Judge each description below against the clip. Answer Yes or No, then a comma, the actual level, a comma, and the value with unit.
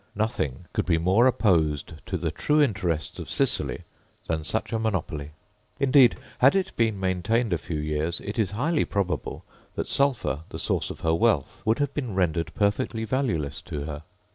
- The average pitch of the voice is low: Yes, low, 100 Hz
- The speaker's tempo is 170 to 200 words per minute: Yes, average, 175 wpm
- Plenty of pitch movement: Yes, wide, 6.5 semitones